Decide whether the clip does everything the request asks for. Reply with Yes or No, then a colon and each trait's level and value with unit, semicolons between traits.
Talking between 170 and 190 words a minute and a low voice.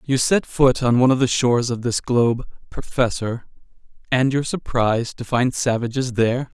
Yes: average, 175 wpm; low, 125 Hz